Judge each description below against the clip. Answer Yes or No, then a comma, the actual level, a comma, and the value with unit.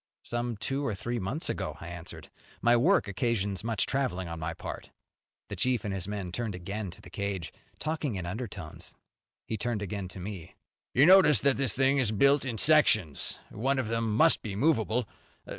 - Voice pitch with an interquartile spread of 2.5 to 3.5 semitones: No, average, 5.1 semitones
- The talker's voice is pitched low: Yes, low, 110 Hz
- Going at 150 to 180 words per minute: No, average, 190 wpm